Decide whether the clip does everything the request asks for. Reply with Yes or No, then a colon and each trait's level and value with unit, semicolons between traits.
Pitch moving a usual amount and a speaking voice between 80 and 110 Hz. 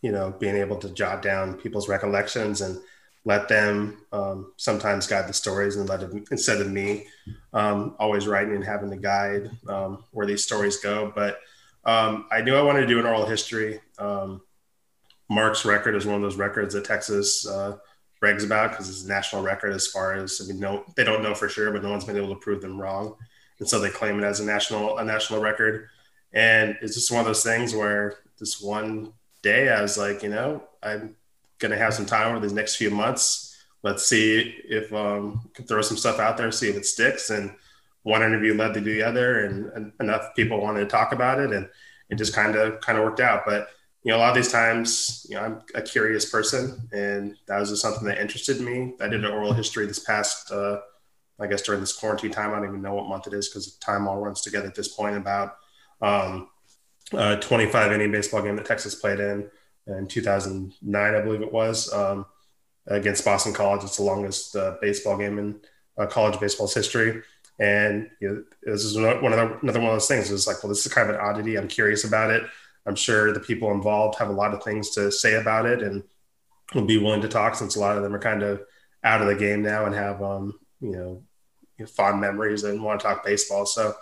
No: narrow, 1.3 semitones; low, 105 Hz